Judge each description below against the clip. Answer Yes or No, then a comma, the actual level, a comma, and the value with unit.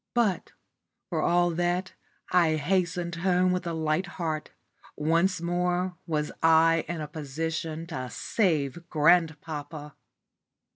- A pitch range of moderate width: No, narrow, 2.3 semitones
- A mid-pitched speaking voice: Yes, medium, 165 Hz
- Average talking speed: No, slow, 115 wpm